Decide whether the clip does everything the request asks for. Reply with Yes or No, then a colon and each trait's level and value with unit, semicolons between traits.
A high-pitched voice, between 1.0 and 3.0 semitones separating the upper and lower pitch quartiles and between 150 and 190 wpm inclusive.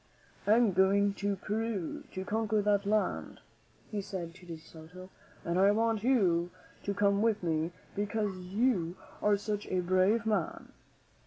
Yes: high, 200 Hz; average, 2.7 semitones; average, 155 wpm